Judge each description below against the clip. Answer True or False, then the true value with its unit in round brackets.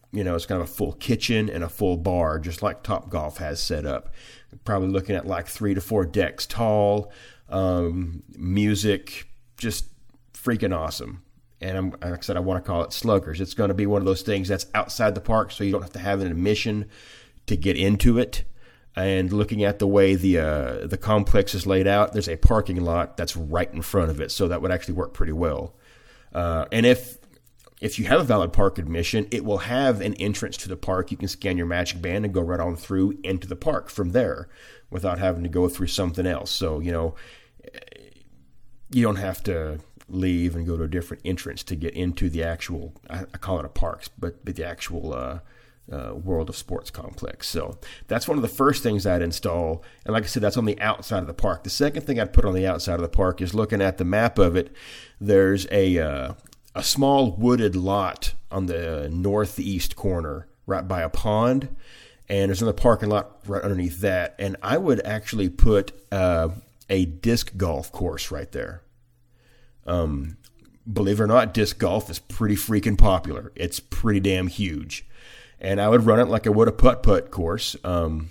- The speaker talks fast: True (210 wpm)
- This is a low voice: True (95 Hz)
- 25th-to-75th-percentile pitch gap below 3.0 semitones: False (3.4 semitones)